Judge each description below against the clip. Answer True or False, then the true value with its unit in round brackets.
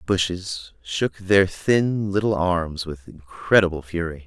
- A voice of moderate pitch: False (90 Hz)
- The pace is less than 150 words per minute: True (140 wpm)